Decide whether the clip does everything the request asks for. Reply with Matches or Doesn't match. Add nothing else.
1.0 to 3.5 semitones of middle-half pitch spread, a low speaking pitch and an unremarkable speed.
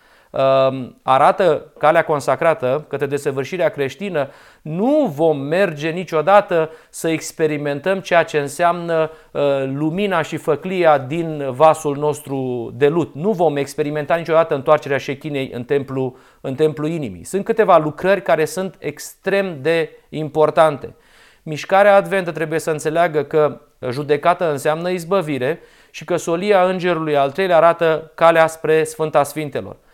Doesn't match